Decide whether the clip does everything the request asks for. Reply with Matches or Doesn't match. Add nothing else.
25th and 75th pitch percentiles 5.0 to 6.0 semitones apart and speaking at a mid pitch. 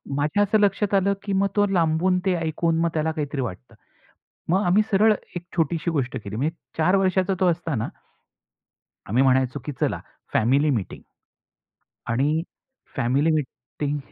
Matches